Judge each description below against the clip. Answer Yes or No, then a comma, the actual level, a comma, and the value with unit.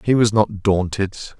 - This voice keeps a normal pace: Yes, average, 170 wpm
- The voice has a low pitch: Yes, low, 105 Hz